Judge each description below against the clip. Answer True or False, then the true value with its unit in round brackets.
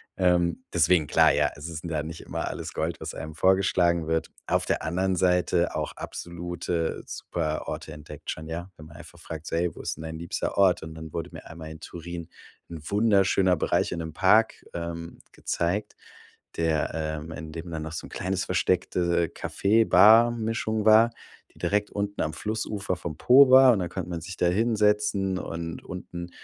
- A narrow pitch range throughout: False (3.2 semitones)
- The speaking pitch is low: True (85 Hz)